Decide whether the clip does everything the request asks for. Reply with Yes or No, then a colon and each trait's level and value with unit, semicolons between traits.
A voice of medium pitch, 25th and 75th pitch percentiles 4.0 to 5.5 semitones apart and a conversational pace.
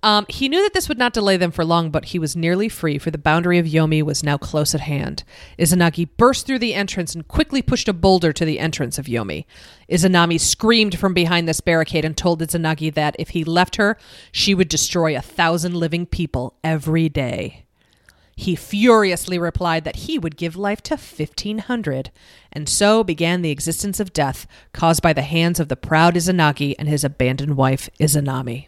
No: medium, 165 Hz; average, 3.5 semitones; average, 195 wpm